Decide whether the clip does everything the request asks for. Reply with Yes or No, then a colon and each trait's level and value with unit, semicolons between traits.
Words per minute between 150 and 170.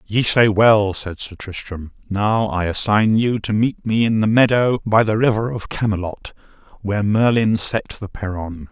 No: average, 180 wpm